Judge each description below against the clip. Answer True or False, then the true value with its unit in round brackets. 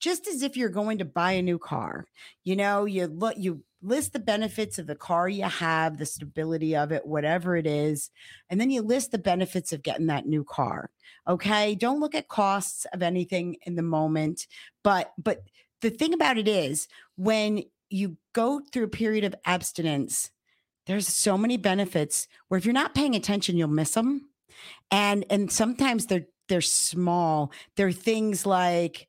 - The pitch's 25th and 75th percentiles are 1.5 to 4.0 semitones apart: False (4.6 semitones)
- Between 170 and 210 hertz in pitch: True (190 Hz)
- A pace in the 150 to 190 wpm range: True (180 wpm)